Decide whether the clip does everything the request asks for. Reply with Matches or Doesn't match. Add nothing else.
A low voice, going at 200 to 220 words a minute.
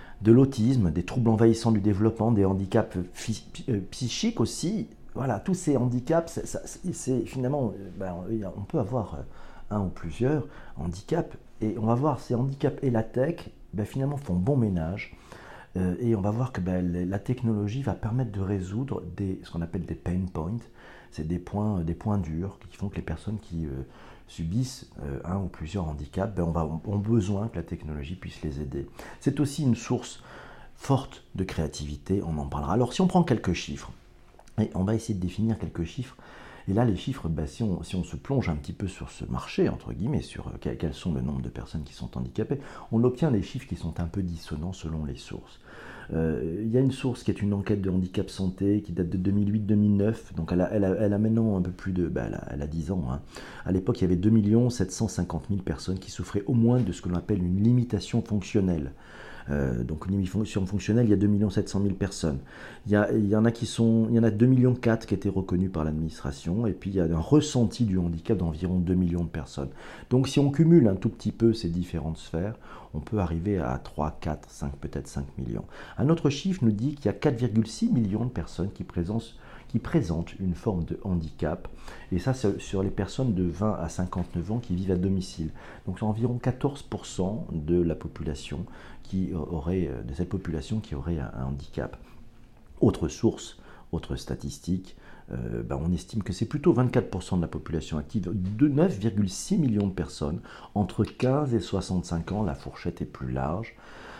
Matches